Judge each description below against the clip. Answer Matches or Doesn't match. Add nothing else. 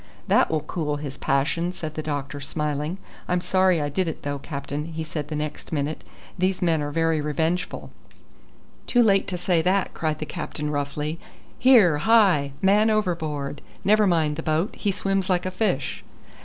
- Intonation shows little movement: Doesn't match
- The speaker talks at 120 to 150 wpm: Doesn't match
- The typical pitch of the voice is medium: Matches